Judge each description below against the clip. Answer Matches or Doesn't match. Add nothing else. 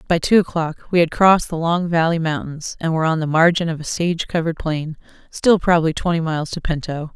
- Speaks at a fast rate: Matches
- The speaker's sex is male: Doesn't match